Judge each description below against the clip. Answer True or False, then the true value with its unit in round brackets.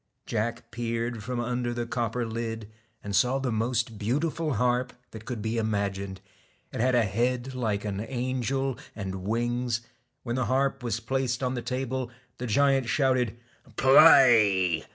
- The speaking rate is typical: True (155 wpm)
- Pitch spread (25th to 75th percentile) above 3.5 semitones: False (2.5 semitones)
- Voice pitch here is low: True (120 Hz)